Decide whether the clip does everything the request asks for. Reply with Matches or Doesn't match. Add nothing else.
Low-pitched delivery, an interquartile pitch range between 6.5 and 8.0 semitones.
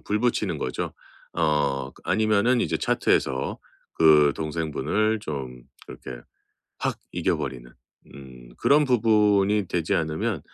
Matches